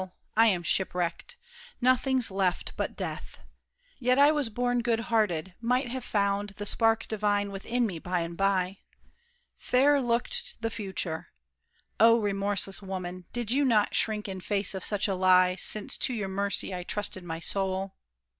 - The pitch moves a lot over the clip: No, average, 3.7 semitones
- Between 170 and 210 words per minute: No, average, 160 wpm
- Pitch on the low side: No, high, 205 Hz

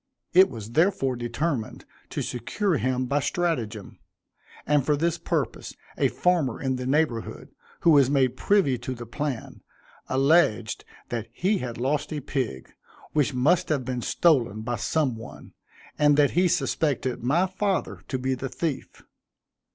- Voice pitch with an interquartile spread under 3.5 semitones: No, average, 4.6 semitones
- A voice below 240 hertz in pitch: Yes, low, 135 Hz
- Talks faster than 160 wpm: No, average, 150 wpm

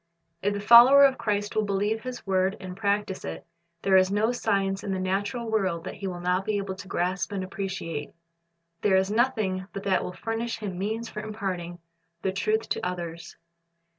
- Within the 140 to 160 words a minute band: No, average, 195 wpm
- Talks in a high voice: Yes, high, 195 Hz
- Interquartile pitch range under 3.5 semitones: Yes, narrow, 2.5 semitones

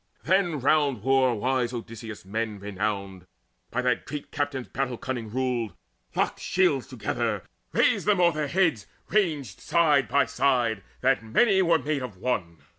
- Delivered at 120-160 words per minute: Yes, average, 145 wpm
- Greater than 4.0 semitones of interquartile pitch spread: Yes, average, 4.9 semitones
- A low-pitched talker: Yes, low, 130 Hz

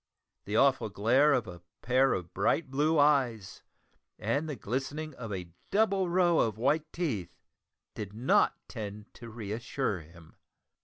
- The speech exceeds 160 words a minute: No, average, 150 wpm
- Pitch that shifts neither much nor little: No, wide, 6.1 semitones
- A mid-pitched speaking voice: No, low, 125 Hz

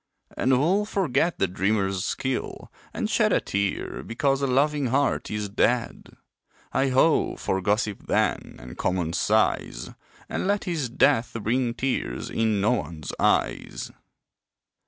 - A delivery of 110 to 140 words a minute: Yes, slow, 135 wpm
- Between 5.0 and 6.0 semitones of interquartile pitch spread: Yes, wide, 5.5 semitones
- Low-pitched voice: Yes, low, 120 Hz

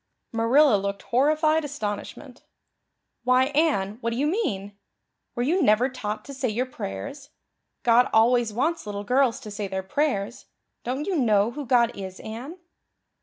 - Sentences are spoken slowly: No, average, 155 wpm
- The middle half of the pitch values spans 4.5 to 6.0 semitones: Yes, average, 5.1 semitones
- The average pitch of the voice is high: Yes, high, 240 Hz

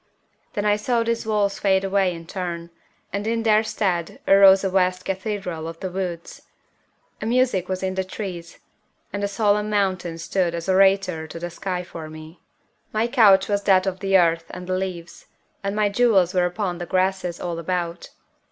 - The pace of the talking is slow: No, average, 185 wpm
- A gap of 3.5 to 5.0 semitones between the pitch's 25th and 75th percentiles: No, narrow, 2.6 semitones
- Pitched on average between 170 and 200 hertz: Yes, high, 190 Hz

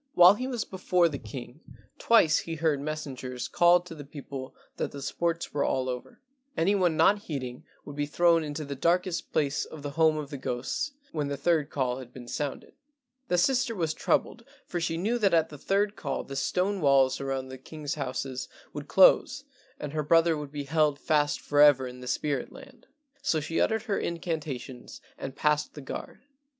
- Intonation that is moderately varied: Yes, average, 3.9 semitones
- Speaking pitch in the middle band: Yes, medium, 150 Hz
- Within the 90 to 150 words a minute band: No, average, 195 wpm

